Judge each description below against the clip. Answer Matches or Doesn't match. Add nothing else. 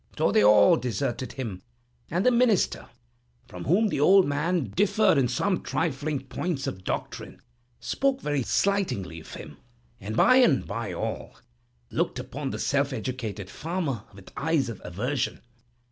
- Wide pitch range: Matches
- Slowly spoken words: Doesn't match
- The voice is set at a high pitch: Doesn't match